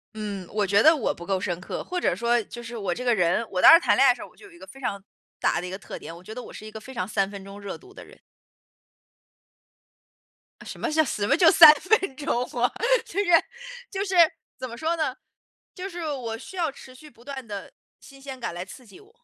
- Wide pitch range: Yes, wide, 7.4 semitones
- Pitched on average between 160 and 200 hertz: No, high, 240 Hz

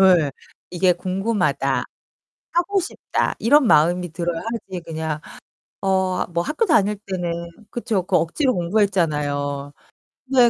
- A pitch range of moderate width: Yes, average, 4.6 semitones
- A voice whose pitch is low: No, medium, 185 Hz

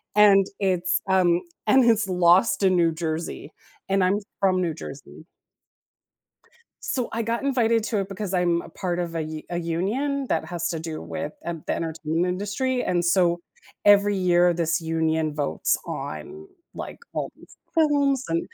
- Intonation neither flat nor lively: Yes, average, 4.0 semitones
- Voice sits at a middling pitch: Yes, medium, 180 Hz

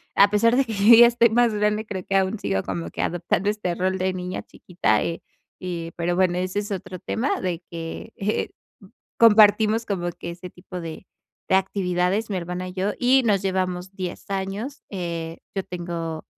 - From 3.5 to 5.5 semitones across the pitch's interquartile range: No, average, 3.0 semitones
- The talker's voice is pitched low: No, medium, 185 Hz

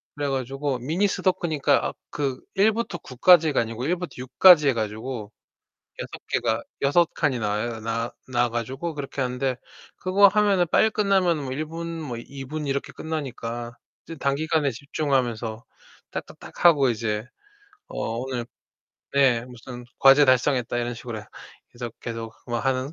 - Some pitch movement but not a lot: Yes, average, 4.7 semitones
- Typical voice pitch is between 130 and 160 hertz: Yes, low, 135 Hz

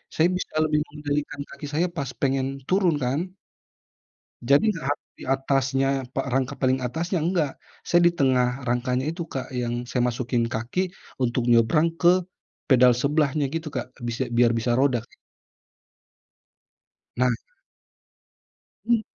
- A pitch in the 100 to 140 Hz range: Yes, low, 135 Hz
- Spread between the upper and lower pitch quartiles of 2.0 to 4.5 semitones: Yes, average, 3.8 semitones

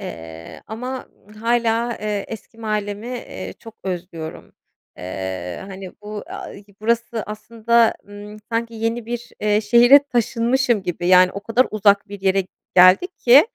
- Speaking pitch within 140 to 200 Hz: No, high, 215 Hz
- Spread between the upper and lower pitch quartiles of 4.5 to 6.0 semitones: No, average, 3.5 semitones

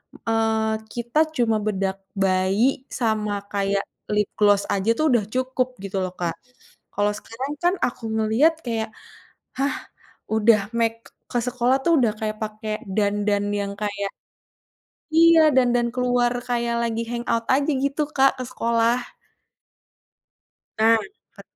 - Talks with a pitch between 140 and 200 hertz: No, high, 225 Hz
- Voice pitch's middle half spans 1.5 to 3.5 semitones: Yes, average, 2.9 semitones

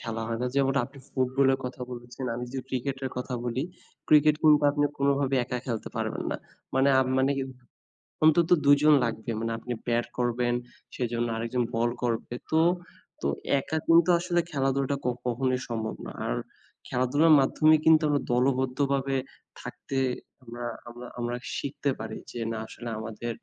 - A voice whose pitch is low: Yes, low, 130 Hz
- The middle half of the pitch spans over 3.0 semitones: No, average, 2.7 semitones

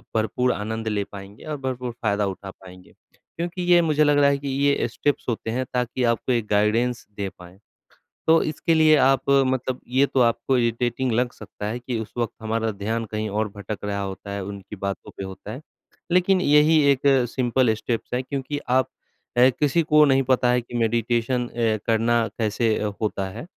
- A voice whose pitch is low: Yes, low, 120 Hz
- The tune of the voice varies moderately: Yes, average, 4.0 semitones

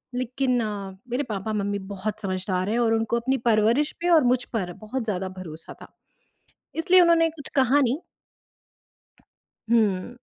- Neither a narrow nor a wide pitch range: Yes, average, 4.5 semitones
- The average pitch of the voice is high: Yes, high, 230 Hz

